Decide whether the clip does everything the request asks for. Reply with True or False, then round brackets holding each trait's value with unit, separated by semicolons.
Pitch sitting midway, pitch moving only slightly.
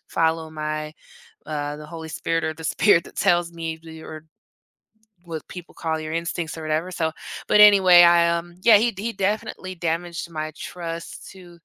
True (165 Hz; 1.8 semitones)